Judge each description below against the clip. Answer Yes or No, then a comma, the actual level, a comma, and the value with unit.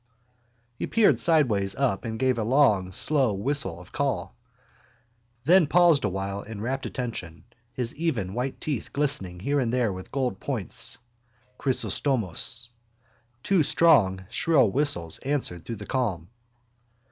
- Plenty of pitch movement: Yes, wide, 6.5 semitones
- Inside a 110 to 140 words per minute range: Yes, slow, 135 wpm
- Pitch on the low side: Yes, low, 125 Hz